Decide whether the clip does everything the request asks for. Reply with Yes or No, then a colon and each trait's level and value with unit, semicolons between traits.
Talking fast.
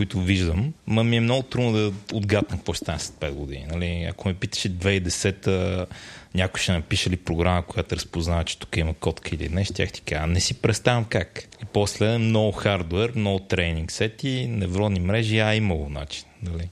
Yes: fast, 190 wpm